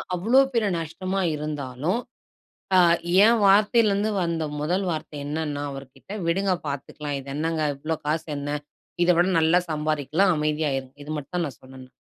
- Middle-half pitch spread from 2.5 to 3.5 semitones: No, average, 4.1 semitones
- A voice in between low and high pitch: Yes, medium, 155 Hz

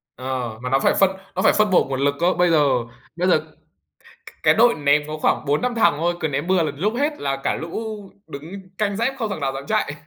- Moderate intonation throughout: No, wide, 5.9 semitones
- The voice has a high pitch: No, medium, 160 Hz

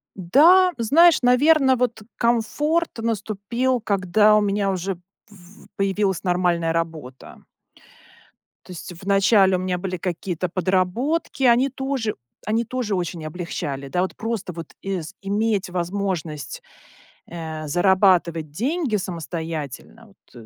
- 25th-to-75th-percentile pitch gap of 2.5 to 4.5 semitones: No, average, 4.9 semitones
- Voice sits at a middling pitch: No, high, 195 Hz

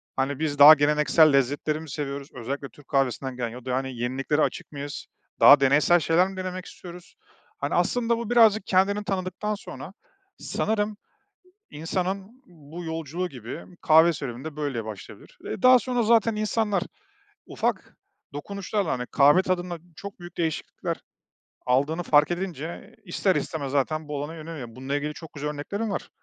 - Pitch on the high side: No, medium, 160 Hz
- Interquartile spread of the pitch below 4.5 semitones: No, average, 5.0 semitones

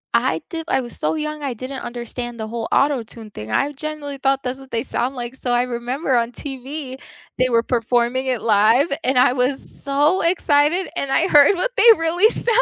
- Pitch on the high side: Yes, very high, 265 Hz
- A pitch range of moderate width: Yes, average, 3.5 semitones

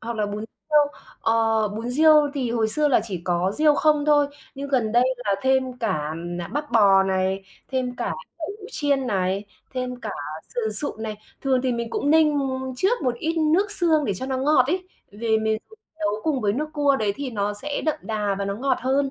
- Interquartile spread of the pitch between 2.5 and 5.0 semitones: No, wide, 5.4 semitones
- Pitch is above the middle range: Yes, very high, 250 Hz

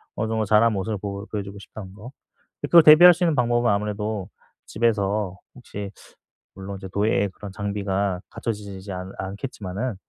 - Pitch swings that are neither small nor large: No, narrow, 2.3 semitones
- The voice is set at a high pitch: No, low, 105 Hz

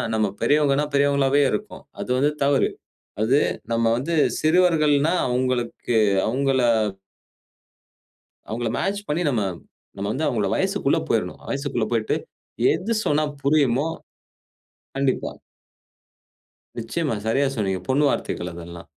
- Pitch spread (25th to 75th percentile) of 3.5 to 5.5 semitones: Yes, average, 4.0 semitones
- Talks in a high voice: No, low, 135 Hz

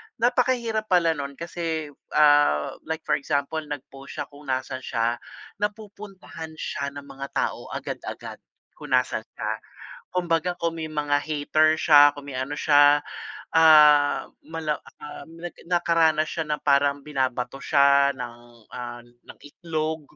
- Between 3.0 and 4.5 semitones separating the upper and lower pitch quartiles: No, narrow, 2.6 semitones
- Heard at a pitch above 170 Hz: No, medium, 150 Hz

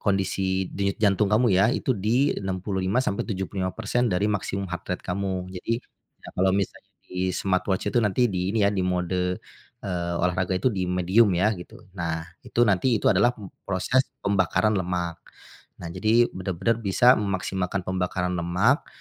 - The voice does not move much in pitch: Yes, narrow, 2.3 semitones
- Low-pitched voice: Yes, very low, 95 Hz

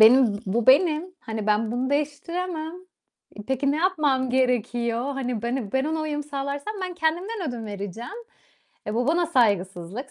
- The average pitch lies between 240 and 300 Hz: Yes, very high, 265 Hz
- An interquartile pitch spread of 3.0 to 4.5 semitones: No, average, 5.3 semitones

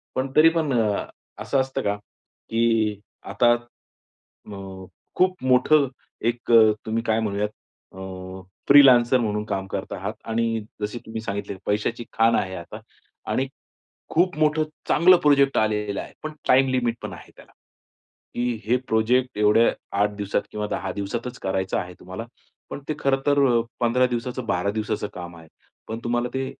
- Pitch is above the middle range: No, low, 115 Hz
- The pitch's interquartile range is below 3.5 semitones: No, average, 3.8 semitones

